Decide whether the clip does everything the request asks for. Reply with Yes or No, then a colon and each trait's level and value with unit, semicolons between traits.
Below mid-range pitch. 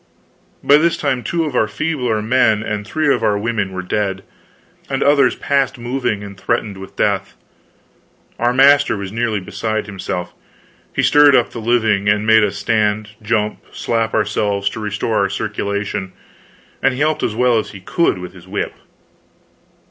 Yes: low, 110 Hz